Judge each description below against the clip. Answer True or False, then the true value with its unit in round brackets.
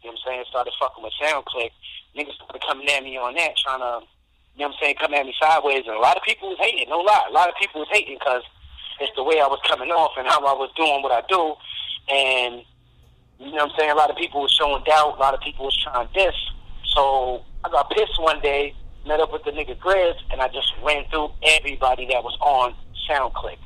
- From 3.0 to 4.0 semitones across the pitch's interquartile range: True (3.5 semitones)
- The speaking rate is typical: False (255 wpm)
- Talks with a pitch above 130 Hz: True (140 Hz)